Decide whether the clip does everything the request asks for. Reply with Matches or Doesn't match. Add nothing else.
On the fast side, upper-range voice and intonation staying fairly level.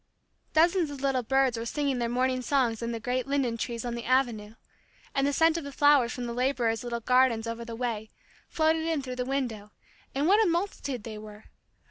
Doesn't match